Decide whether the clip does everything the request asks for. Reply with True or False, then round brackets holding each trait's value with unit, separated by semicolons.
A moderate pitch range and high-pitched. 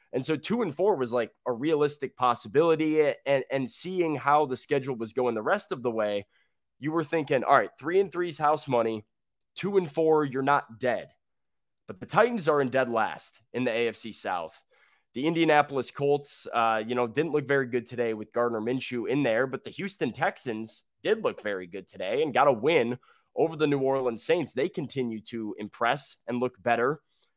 False (4.7 semitones; 135 Hz)